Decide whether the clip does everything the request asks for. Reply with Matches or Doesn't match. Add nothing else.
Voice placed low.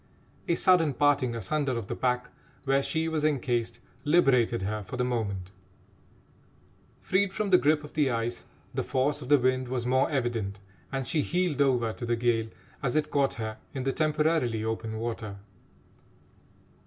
Matches